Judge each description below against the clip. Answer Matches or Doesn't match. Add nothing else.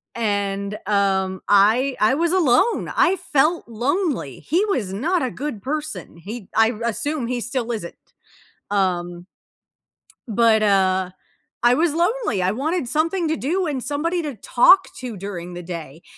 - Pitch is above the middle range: Matches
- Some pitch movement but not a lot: Doesn't match